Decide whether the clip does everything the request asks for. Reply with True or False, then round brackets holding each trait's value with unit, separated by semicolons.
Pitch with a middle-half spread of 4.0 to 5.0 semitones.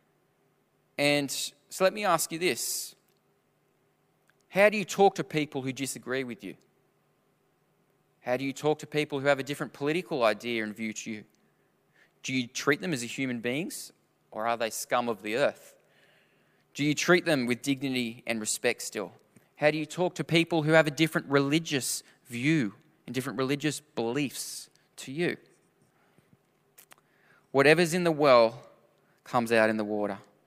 True (4.7 semitones)